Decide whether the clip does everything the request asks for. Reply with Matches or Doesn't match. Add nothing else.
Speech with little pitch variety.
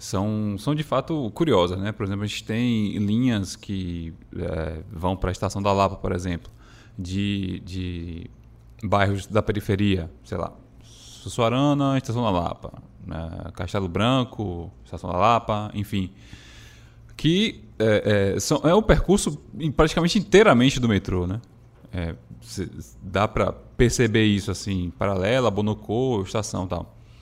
Doesn't match